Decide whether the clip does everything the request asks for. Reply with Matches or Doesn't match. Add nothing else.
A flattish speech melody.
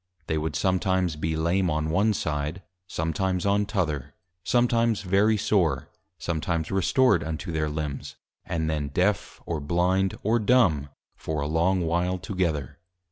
Doesn't match